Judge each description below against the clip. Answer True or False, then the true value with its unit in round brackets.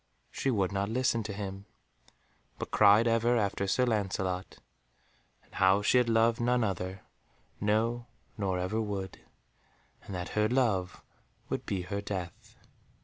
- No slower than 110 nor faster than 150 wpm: True (145 wpm)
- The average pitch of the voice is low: True (105 Hz)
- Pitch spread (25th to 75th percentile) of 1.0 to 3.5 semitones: True (3.2 semitones)